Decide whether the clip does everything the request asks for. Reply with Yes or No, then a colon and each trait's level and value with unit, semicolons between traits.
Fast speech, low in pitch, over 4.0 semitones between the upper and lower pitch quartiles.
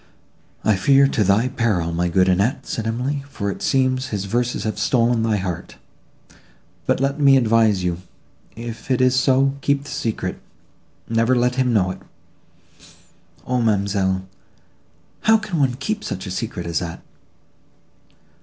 No: average, 150 wpm; low, 115 Hz; average, 5.1 semitones